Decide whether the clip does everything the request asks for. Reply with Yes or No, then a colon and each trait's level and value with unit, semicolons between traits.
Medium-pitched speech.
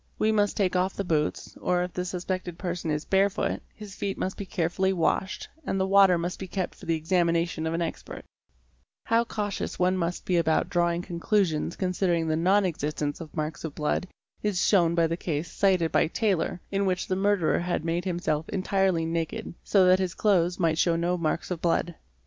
Yes: medium, 180 Hz